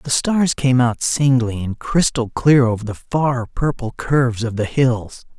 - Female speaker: No, male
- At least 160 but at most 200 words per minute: Yes, average, 180 wpm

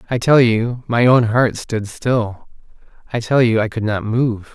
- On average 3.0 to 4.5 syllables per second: Yes, 4.1 syllables/s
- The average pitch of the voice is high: No, low, 115 Hz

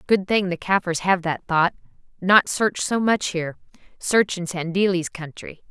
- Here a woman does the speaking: Yes, female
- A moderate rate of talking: Yes, average, 170 wpm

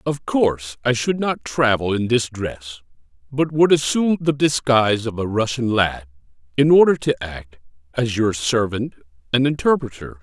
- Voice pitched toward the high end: No, low, 120 Hz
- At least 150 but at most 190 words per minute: Yes, average, 160 wpm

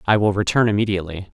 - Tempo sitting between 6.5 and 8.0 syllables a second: Yes, 7.5 syllables/s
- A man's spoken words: Yes, male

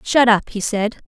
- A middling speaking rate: No, fast, 225 wpm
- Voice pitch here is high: Yes, high, 220 Hz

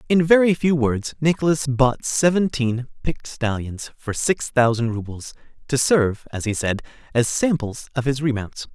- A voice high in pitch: No, low, 135 Hz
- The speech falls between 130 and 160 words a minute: Yes, average, 150 wpm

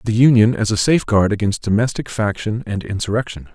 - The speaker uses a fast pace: No, average, 170 wpm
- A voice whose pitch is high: No, low, 110 Hz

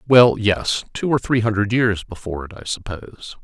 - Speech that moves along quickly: No, average, 190 wpm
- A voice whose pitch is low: Yes, low, 105 Hz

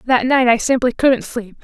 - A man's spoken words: No, female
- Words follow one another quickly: Yes, fast, 220 wpm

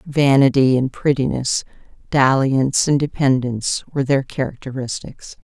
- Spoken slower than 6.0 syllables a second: Yes, 4.9 syllables/s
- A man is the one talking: No, female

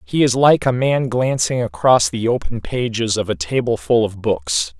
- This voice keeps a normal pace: Yes, average, 190 wpm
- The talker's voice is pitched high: No, low, 110 Hz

